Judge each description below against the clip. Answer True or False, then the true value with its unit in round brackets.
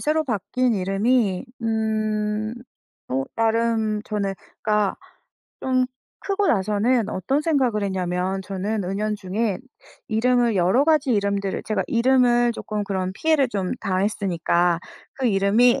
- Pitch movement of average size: True (3.8 semitones)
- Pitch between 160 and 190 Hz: False (215 Hz)